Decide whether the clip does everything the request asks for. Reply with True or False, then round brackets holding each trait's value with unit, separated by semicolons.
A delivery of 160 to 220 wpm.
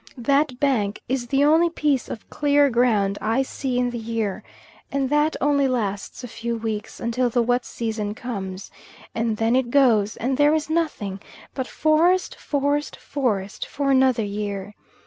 True (165 wpm)